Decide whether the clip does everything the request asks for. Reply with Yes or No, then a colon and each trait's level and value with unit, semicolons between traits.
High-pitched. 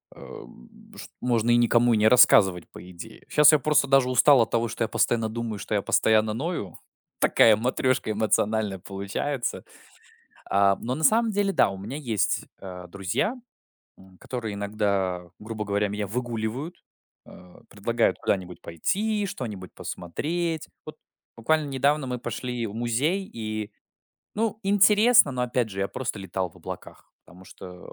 No: low, 115 Hz